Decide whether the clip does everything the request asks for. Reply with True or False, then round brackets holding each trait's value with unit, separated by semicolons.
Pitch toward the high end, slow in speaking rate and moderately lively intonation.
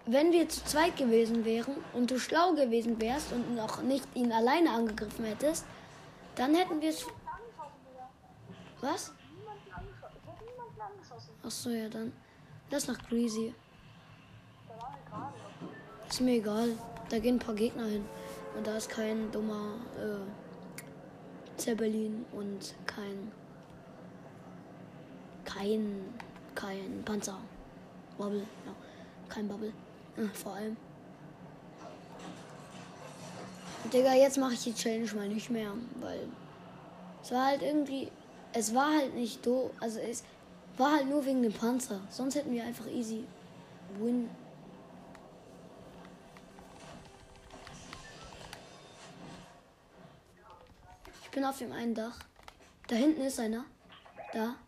True (235 Hz; 110 wpm; 3.3 semitones)